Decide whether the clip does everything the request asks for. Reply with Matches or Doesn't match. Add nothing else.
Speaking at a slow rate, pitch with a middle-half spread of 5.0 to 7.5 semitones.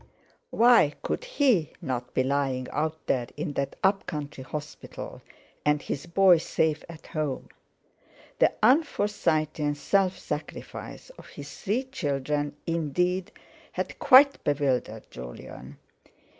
Matches